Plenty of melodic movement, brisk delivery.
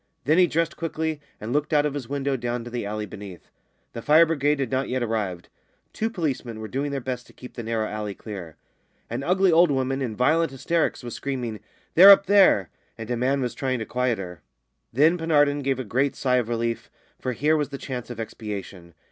No: average, 4.5 semitones; fast, 215 wpm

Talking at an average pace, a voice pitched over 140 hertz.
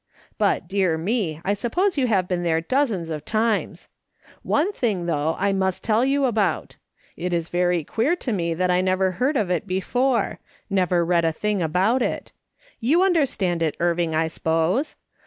Yes: average, 175 wpm; high, 190 Hz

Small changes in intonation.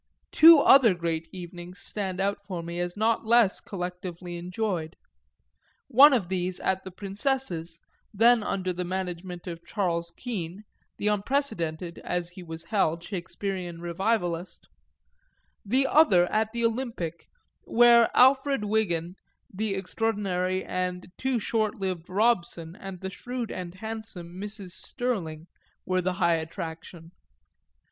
No: average, 4.0 semitones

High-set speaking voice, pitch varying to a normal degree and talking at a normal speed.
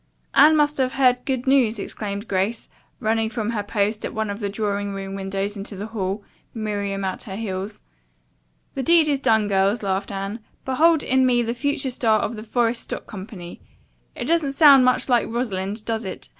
Yes: high, 220 Hz; average, 4.1 semitones; average, 190 wpm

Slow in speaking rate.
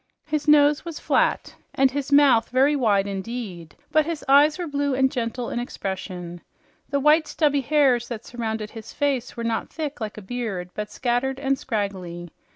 No: average, 175 wpm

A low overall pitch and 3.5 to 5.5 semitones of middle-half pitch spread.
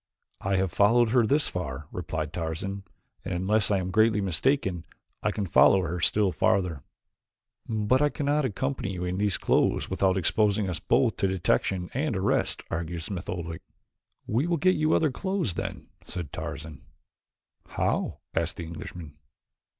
Yes: very low, 95 Hz; average, 4.7 semitones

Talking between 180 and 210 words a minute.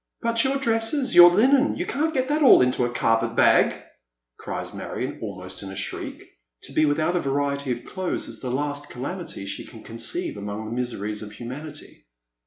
Yes: average, 195 wpm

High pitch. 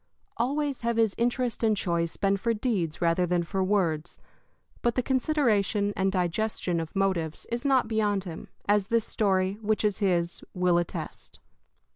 Yes: high, 200 Hz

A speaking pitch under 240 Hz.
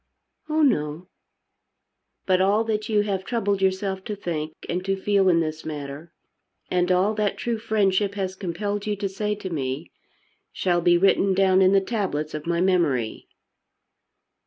Yes: high, 190 Hz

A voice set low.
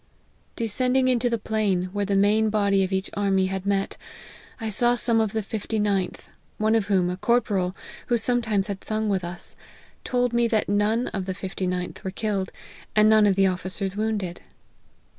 No: high, 205 Hz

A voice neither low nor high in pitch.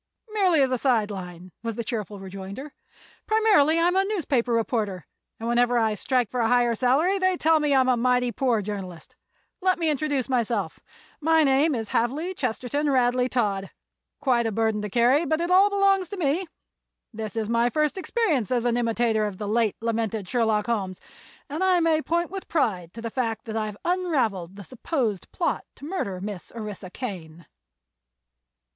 No: high, 245 Hz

